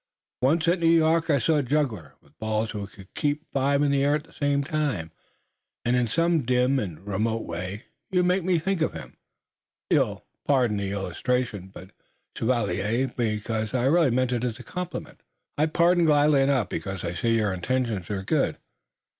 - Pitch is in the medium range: No, low, 125 Hz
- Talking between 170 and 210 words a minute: Yes, average, 180 wpm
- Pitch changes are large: Yes, wide, 6.1 semitones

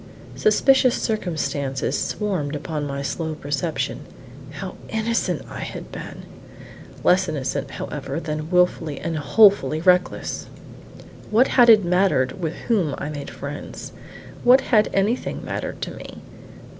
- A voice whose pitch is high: No, medium, 165 Hz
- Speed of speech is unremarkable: No, slow, 125 wpm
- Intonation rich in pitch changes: Yes, wide, 6.3 semitones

